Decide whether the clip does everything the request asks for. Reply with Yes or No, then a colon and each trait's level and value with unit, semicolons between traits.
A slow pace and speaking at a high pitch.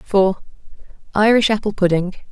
Yes: slow, 80 wpm; high, 200 Hz